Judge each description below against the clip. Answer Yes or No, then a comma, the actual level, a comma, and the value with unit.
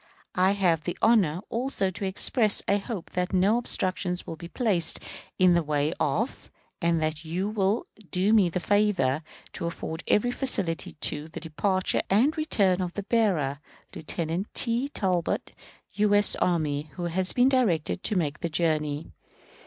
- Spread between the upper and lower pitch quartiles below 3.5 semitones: No, average, 4.2 semitones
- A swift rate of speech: No, average, 160 wpm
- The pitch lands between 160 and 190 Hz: Yes, medium, 185 Hz